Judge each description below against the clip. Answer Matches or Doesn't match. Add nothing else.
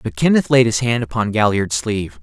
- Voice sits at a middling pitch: Doesn't match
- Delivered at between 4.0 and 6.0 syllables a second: Matches